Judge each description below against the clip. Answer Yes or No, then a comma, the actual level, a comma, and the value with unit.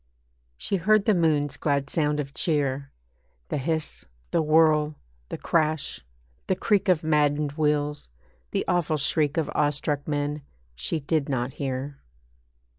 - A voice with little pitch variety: Yes, narrow, 1.9 semitones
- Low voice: No, medium, 150 Hz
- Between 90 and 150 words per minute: Yes, slow, 135 wpm